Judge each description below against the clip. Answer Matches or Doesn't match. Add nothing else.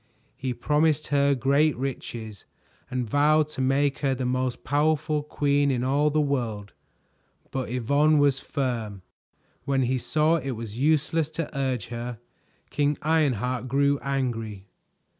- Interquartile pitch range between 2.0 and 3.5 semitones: Matches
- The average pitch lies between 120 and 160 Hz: Matches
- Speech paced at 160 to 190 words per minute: Doesn't match